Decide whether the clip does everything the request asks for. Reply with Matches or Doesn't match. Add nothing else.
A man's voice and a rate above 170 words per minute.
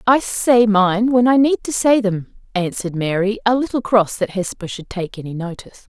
Doesn't match